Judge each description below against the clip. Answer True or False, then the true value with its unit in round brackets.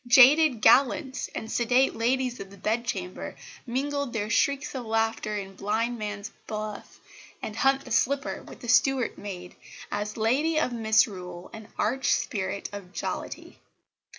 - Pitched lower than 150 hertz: False (230 Hz)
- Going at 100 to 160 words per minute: True (145 wpm)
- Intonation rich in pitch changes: False (4.0 semitones)